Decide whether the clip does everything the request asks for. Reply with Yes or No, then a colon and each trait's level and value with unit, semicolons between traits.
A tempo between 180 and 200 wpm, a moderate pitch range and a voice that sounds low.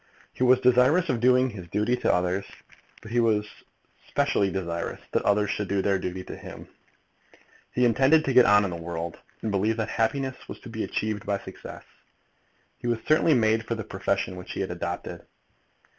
Yes: average, 190 wpm; average, 4.3 semitones; low, 110 Hz